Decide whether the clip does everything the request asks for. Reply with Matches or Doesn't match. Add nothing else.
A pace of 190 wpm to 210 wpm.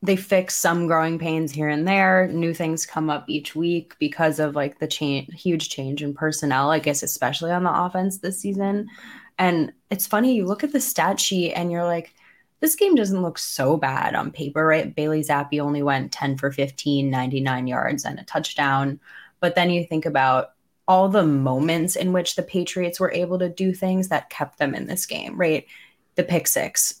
Matches